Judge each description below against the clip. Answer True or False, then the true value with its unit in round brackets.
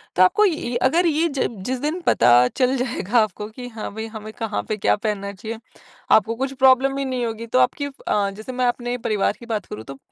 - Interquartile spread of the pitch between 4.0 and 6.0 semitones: False (3.4 semitones)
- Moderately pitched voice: False (235 Hz)